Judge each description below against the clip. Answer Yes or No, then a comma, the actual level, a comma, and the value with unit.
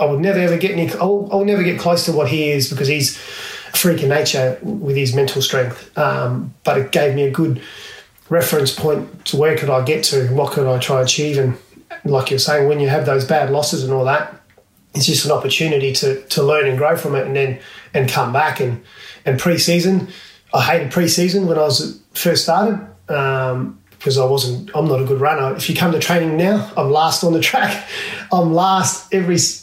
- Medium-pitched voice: Yes, medium, 150 Hz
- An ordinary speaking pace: No, fast, 220 wpm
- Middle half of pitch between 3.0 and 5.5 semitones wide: Yes, average, 4.0 semitones